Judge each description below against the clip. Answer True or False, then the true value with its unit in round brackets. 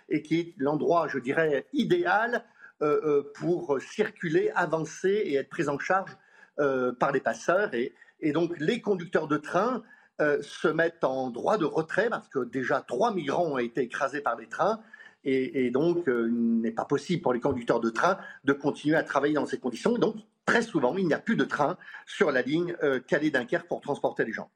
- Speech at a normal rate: True (205 wpm)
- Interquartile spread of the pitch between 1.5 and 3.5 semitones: False (5.0 semitones)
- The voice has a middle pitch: True (155 Hz)